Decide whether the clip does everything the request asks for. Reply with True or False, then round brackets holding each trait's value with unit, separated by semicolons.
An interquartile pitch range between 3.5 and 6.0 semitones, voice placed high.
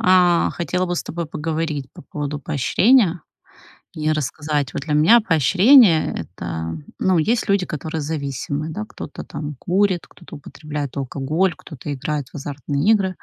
False (4.0 semitones; 155 Hz)